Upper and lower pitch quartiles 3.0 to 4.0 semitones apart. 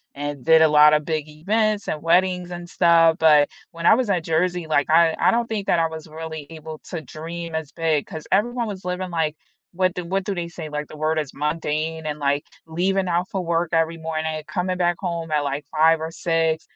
No: narrow, 2.4 semitones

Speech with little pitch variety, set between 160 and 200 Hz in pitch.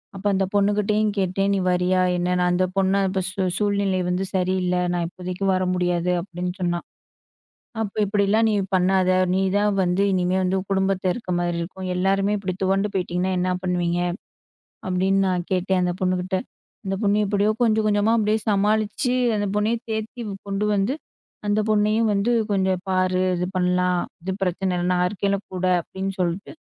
Yes: narrow, 2.0 semitones; high, 190 Hz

